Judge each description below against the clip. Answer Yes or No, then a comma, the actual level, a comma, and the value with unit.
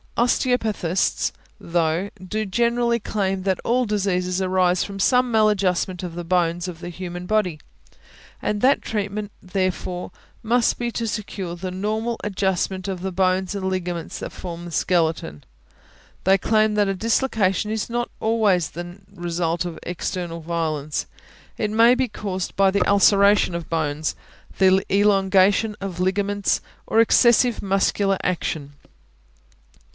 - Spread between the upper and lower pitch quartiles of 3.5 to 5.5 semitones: No, average, 3.0 semitones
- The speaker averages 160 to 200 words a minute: No, average, 140 wpm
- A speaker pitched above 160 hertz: Yes, high, 190 Hz